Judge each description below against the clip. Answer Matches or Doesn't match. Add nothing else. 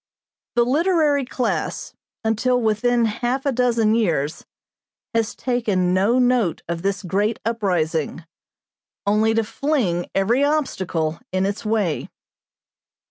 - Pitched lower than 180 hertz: Doesn't match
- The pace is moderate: Doesn't match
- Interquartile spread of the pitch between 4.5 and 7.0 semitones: Matches